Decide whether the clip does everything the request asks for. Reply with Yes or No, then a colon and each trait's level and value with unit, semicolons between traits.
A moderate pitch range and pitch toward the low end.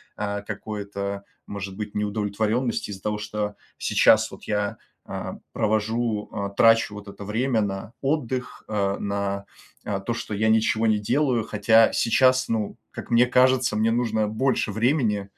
No: narrow, 2.3 semitones; low, 110 Hz